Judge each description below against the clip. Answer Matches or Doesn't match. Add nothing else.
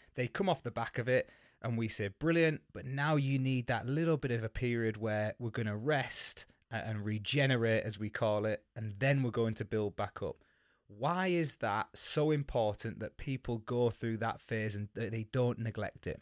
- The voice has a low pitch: Matches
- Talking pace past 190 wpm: Matches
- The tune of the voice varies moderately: Matches